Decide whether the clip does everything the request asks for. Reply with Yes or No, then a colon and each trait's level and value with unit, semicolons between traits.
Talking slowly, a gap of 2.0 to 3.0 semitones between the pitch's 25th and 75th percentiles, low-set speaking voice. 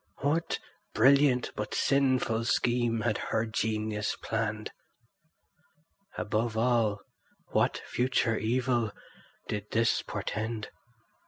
Yes: slow, 90 wpm; narrow, 2.4 semitones; low, 115 Hz